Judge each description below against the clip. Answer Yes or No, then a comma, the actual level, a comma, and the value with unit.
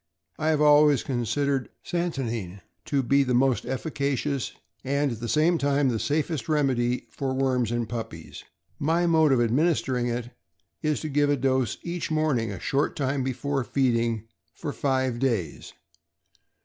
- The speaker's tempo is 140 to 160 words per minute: Yes, average, 150 wpm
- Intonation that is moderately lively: Yes, average, 3.4 semitones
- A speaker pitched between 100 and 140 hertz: Yes, low, 135 Hz